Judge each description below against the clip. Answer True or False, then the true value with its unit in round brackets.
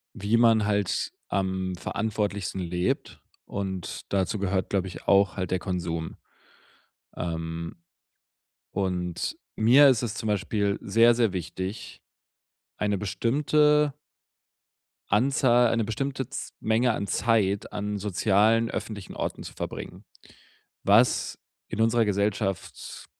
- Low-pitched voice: True (105 Hz)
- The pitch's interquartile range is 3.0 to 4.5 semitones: True (3.4 semitones)